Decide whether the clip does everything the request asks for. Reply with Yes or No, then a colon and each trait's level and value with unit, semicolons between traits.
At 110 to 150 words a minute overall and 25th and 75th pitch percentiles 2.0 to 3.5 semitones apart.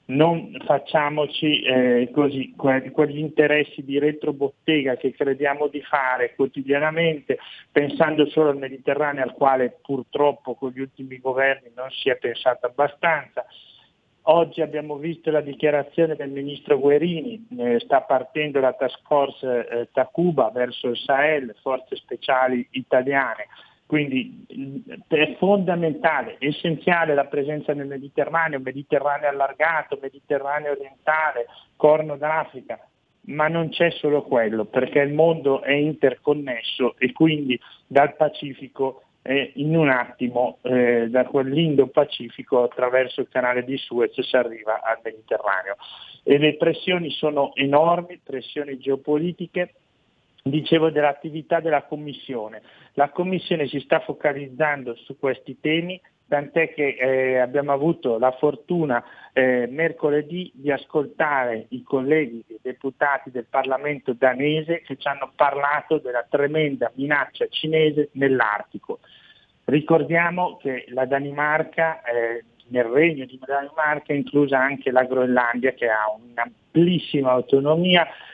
Yes: average, 125 wpm; average, 3.0 semitones